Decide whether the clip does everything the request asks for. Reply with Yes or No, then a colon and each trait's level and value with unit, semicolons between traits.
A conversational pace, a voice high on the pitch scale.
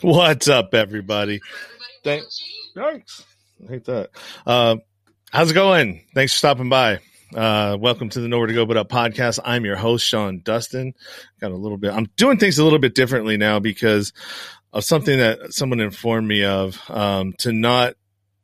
No: average, 175 wpm; low, 115 Hz